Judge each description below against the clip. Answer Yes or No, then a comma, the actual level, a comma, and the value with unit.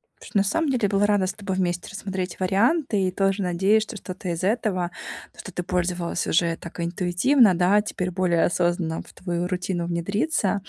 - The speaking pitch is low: No, medium, 185 Hz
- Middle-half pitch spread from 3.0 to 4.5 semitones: No, narrow, 2.6 semitones